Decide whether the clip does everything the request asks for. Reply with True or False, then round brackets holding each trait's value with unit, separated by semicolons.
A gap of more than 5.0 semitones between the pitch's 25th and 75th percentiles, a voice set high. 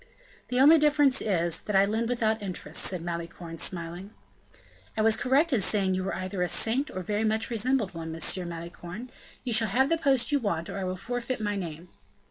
True (5.6 semitones; 205 Hz)